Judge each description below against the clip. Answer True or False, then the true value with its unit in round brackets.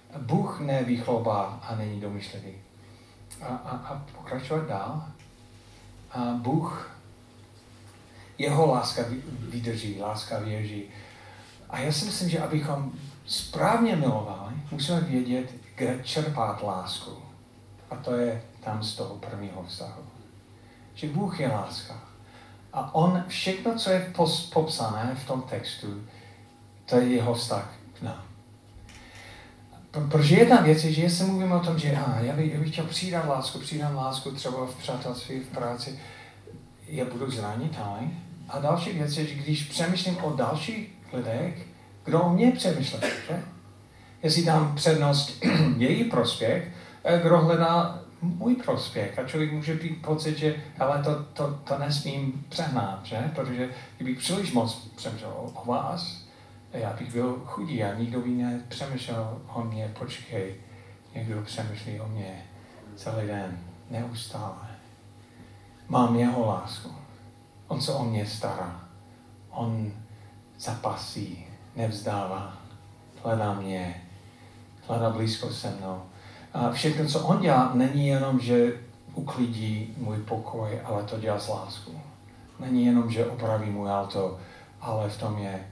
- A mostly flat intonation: False (4.7 semitones)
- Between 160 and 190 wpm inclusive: False (135 wpm)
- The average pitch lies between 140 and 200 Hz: False (120 Hz)